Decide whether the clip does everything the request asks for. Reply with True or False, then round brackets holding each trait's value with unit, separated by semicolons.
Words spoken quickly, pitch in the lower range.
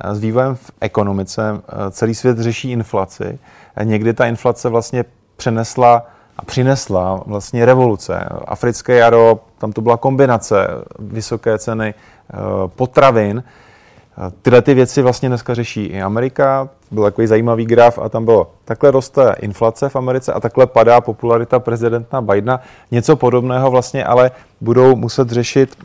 False (135 wpm; 120 Hz)